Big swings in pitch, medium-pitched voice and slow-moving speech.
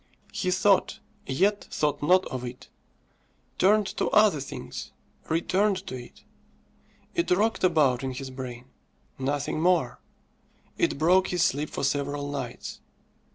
Yes: wide, 6.0 semitones; medium, 150 Hz; slow, 130 wpm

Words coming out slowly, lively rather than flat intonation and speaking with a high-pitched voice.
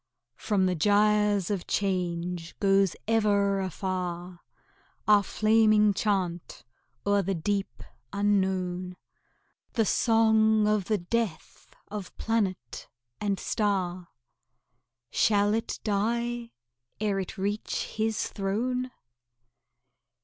No: slow, 95 wpm; narrow, 2.5 semitones; high, 200 Hz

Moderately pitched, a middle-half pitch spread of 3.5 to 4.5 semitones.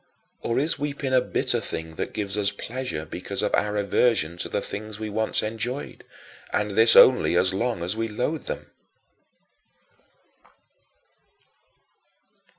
No: low, 110 Hz; average, 3.9 semitones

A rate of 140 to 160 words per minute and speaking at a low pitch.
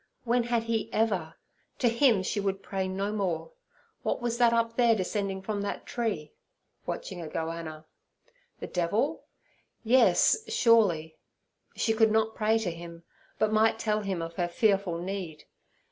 No: average, 155 wpm; high, 210 Hz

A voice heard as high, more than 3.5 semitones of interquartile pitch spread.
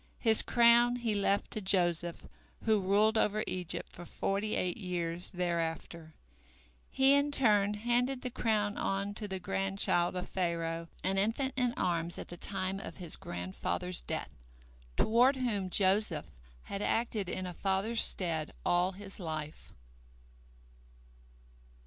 Yes: high, 195 Hz; average, 4.0 semitones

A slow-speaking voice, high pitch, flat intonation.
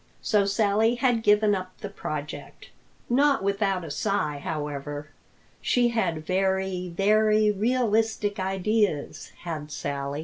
No: slow, 115 wpm; high, 195 Hz; average, 4.9 semitones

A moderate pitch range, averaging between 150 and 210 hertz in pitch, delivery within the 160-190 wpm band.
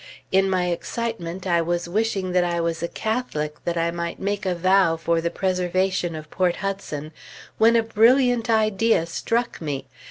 Yes: average, 4.2 semitones; medium, 185 Hz; average, 170 wpm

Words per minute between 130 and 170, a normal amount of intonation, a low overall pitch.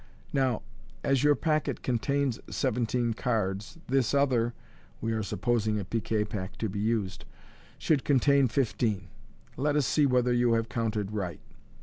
Yes: average, 155 wpm; average, 4.0 semitones; low, 120 Hz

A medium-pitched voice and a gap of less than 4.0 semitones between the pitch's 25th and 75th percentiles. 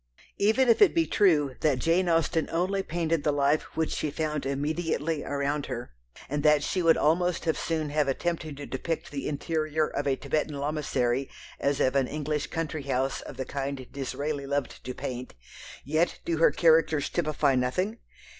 Yes: medium, 150 Hz; average, 2.8 semitones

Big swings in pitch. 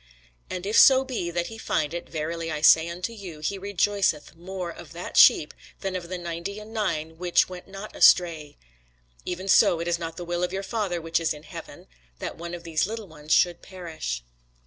No: average, 2.8 semitones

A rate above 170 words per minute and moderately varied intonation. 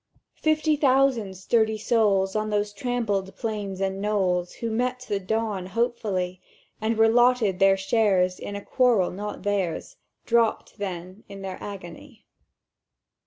No: slow, 135 wpm; average, 3.2 semitones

